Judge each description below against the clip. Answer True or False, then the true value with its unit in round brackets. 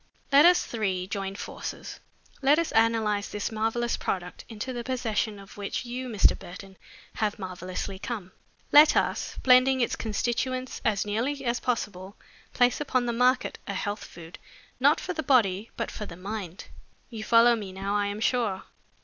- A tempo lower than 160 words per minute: False (170 wpm)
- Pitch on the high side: True (220 Hz)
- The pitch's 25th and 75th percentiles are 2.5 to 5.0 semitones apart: True (4.0 semitones)